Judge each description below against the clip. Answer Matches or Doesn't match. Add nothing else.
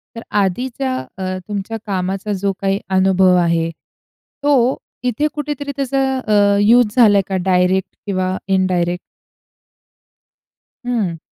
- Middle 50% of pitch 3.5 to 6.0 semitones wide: Matches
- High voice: Matches